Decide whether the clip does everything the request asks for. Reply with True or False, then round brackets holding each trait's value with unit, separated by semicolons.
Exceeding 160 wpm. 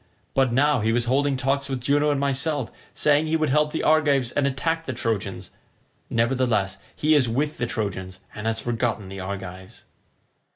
True (175 wpm)